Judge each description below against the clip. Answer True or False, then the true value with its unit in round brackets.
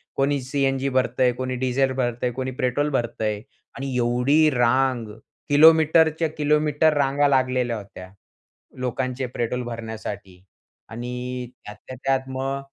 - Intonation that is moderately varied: False (2.2 semitones)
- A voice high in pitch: False (130 Hz)